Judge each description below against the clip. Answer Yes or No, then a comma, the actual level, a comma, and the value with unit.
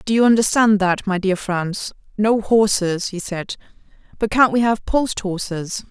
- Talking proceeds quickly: No, average, 165 wpm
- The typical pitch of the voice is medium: No, high, 205 Hz